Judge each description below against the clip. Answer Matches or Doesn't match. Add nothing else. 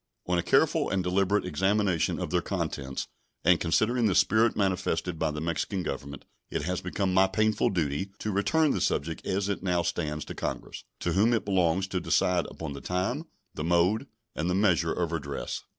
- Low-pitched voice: Matches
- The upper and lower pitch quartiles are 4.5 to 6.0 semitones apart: Doesn't match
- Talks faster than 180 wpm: Matches